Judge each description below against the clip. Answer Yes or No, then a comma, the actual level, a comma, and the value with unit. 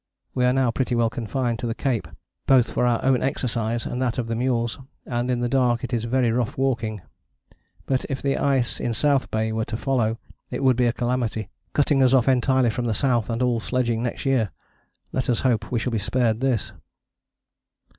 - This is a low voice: Yes, low, 120 Hz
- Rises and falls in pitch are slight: Yes, narrow, 2.1 semitones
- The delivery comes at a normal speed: No, fast, 210 wpm